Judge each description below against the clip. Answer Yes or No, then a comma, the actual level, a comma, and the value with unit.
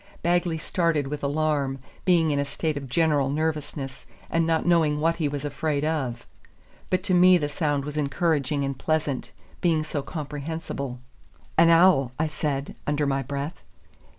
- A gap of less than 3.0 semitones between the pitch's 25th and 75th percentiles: Yes, narrow, 2.6 semitones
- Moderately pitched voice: Yes, medium, 150 Hz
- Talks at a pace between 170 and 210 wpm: No, average, 160 wpm